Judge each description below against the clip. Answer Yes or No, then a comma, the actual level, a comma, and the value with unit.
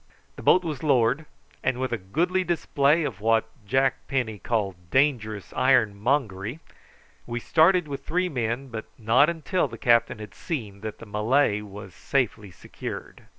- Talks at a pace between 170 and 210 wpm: No, average, 150 wpm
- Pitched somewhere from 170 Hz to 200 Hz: No, low, 120 Hz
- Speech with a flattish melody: No, average, 5.3 semitones